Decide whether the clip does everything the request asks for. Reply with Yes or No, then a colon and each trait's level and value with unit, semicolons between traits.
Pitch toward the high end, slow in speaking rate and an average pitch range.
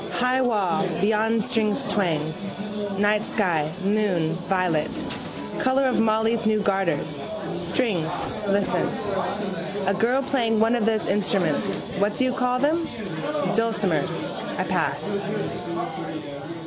Yes: high, 210 Hz; slow, 110 wpm; average, 3.6 semitones